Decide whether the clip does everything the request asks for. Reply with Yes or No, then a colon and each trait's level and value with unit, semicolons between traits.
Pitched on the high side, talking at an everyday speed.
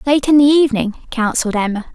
Yes: very high, 255 Hz; average, 185 wpm